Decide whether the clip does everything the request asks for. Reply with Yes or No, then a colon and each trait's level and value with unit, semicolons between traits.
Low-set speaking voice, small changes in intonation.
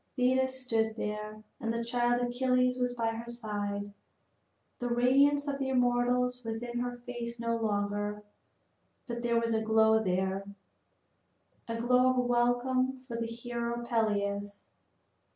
No: high, 235 Hz; narrow, 2.0 semitones